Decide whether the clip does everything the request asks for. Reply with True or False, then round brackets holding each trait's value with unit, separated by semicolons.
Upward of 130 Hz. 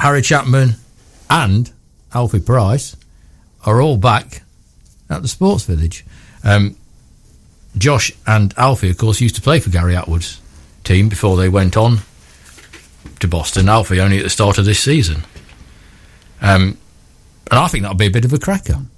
False (100 Hz)